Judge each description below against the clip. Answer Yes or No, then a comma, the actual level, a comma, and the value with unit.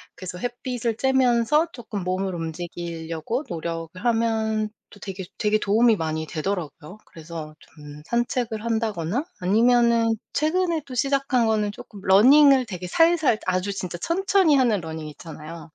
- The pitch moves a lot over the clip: Yes, wide, 6.1 semitones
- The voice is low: No, high, 215 Hz